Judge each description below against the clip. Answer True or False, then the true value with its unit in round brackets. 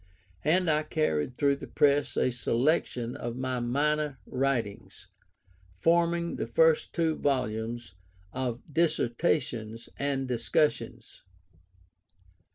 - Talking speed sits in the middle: False (100 wpm)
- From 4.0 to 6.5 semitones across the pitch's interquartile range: True (4.3 semitones)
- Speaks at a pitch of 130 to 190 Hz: True (135 Hz)